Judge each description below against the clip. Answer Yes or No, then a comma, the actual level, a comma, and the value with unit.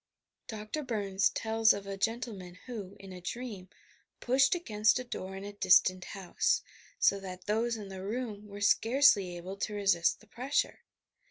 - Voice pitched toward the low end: No, high, 205 Hz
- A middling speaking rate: Yes, average, 165 wpm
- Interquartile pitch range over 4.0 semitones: No, average, 3.2 semitones